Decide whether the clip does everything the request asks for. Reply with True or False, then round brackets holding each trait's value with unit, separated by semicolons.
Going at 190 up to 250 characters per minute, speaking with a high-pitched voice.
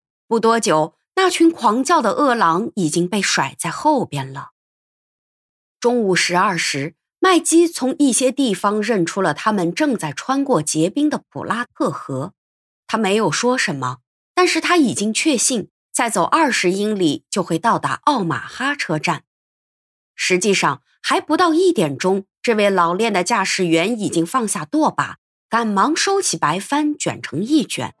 True (230 characters per minute; 215 Hz)